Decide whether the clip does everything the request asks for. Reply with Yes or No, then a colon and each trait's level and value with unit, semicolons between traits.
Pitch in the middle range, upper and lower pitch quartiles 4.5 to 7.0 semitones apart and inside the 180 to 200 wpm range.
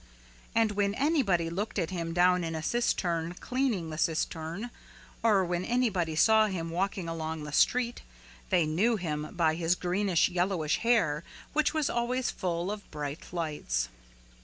No: medium, 180 Hz; average, 4.9 semitones; average, 155 wpm